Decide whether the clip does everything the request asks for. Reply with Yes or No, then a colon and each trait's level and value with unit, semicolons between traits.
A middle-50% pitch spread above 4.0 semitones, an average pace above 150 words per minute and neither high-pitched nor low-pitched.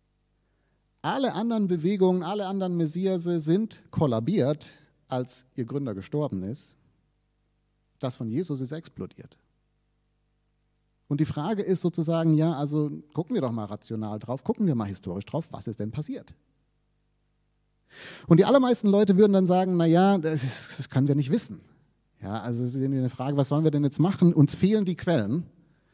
Yes: average, 5.2 semitones; average, 160 wpm; medium, 150 Hz